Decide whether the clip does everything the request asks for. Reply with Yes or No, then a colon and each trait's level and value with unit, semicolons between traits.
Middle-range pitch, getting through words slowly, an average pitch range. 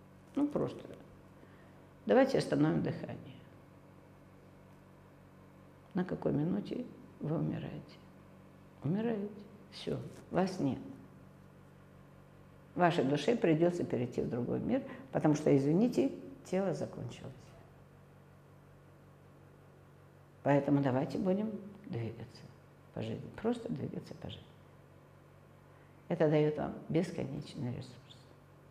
No: medium, 150 Hz; slow, 80 wpm; wide, 6.5 semitones